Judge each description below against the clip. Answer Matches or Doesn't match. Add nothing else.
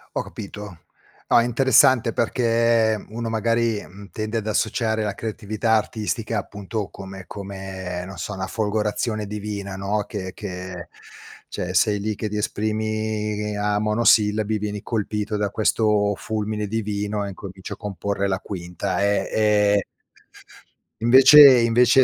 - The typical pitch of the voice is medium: Doesn't match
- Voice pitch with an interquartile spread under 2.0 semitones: Matches